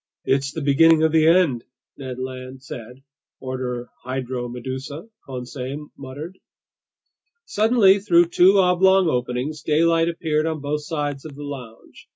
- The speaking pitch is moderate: Yes, medium, 145 Hz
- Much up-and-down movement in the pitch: No, average, 4.1 semitones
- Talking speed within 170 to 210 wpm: No, slow, 135 wpm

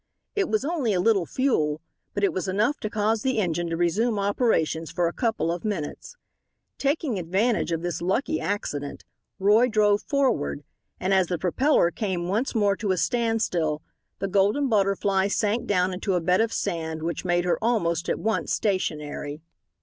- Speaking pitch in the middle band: No, high, 195 Hz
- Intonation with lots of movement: No, average, 4.5 semitones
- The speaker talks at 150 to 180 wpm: Yes, average, 175 wpm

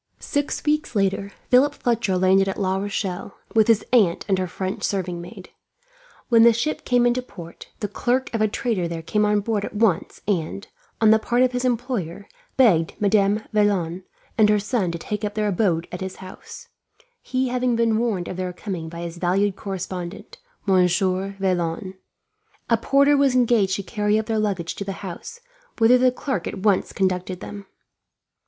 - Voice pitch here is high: Yes, high, 205 Hz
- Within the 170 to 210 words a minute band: Yes, average, 185 wpm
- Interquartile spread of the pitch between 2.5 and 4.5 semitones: Yes, average, 3.8 semitones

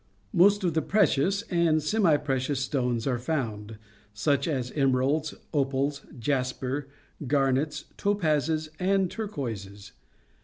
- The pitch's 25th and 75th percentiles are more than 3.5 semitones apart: Yes, average, 4.1 semitones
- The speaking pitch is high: No, medium, 145 Hz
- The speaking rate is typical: No, slow, 110 wpm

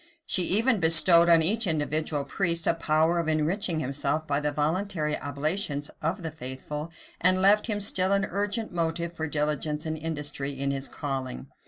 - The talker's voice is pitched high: No, medium, 160 Hz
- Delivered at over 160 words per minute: Yes, average, 170 wpm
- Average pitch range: Yes, average, 3.6 semitones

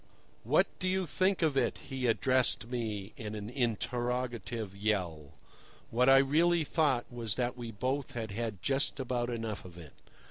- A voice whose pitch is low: Yes, low, 120 Hz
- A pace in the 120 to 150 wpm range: No, average, 165 wpm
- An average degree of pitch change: Yes, average, 3.8 semitones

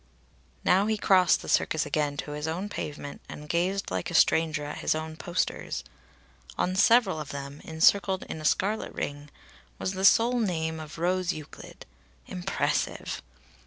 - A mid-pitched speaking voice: Yes, medium, 160 Hz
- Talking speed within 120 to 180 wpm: Yes, average, 160 wpm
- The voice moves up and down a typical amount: Yes, average, 4.0 semitones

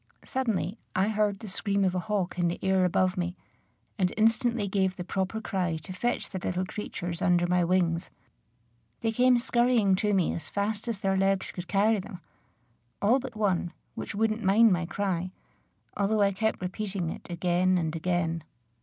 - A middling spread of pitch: Yes, average, 3.1 semitones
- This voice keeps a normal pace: Yes, average, 180 wpm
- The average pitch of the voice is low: No, high, 190 Hz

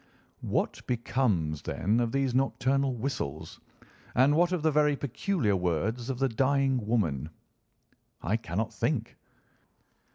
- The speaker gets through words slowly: Yes, slow, 125 wpm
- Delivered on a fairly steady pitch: No, average, 4.7 semitones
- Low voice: Yes, low, 125 Hz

